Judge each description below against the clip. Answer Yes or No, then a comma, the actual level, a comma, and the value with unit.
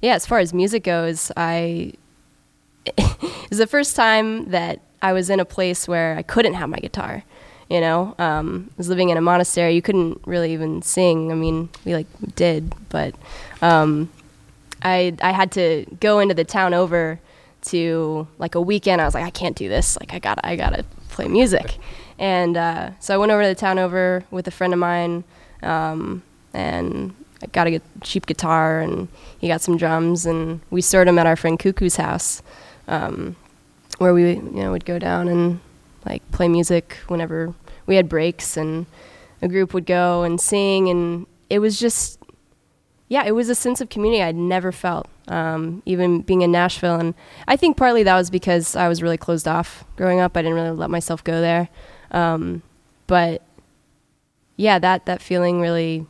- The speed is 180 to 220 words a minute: Yes, average, 185 wpm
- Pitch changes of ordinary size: No, narrow, 2.0 semitones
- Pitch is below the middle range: No, medium, 175 Hz